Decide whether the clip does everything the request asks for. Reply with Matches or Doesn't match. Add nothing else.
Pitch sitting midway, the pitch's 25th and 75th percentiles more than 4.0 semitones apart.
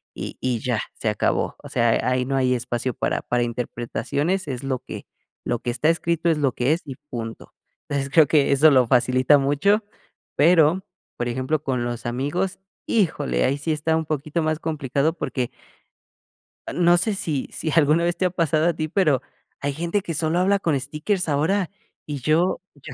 Matches